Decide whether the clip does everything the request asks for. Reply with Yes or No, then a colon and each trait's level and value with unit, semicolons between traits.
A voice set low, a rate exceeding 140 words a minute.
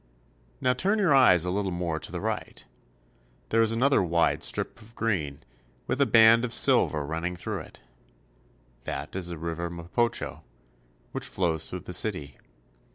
Yes: very low, 90 Hz; average, 165 wpm